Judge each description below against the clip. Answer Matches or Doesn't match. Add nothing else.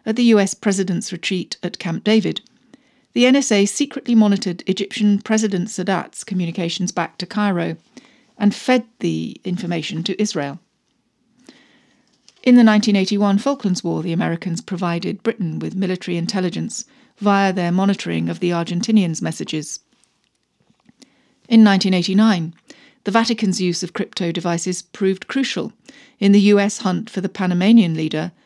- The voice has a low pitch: Doesn't match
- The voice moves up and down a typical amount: Matches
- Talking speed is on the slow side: Matches